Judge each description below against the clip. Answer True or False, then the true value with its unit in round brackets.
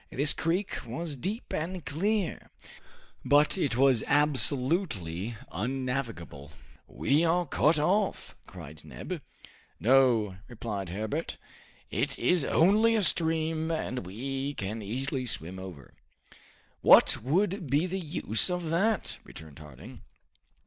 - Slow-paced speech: True (115 wpm)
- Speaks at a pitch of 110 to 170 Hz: True (135 Hz)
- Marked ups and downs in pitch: True (7.5 semitones)